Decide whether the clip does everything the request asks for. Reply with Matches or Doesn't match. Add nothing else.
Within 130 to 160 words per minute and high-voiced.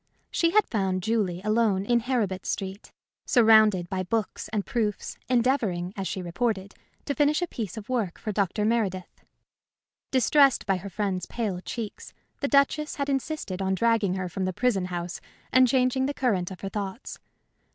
Doesn't match